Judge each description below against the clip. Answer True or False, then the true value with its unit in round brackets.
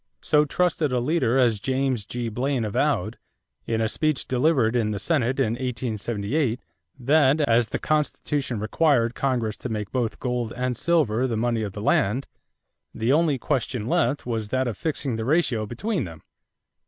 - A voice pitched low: True (125 Hz)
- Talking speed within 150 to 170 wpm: True (165 wpm)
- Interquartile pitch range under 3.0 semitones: False (4.1 semitones)